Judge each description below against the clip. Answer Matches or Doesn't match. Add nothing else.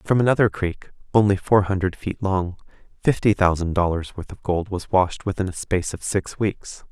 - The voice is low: Matches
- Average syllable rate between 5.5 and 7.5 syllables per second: Doesn't match